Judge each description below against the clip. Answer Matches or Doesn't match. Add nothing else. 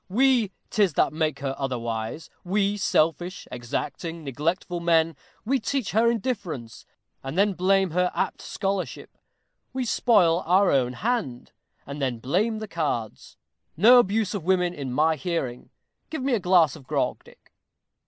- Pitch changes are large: Matches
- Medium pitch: Matches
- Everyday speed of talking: Matches